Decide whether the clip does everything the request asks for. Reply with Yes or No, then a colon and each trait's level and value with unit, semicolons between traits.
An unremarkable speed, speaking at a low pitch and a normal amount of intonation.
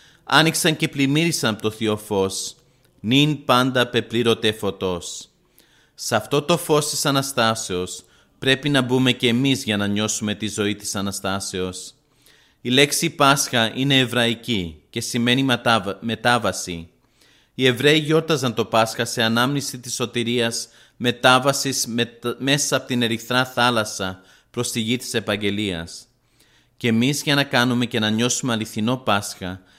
Yes: average, 135 wpm; low, 120 Hz; average, 3.6 semitones